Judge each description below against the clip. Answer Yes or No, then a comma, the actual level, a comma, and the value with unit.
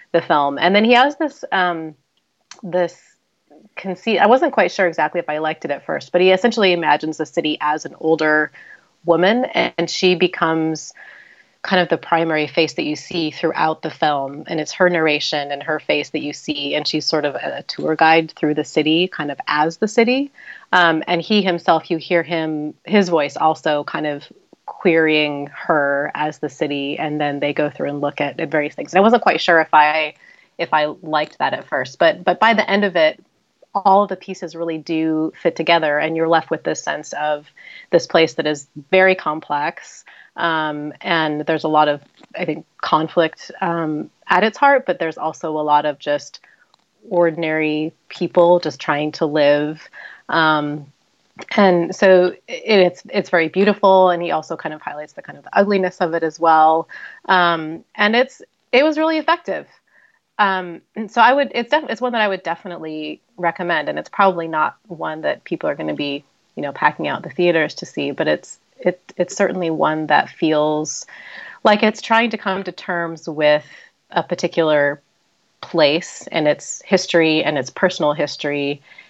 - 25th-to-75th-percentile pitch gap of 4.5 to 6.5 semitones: No, average, 3.2 semitones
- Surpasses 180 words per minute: Yes, average, 190 wpm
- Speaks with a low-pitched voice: No, medium, 165 Hz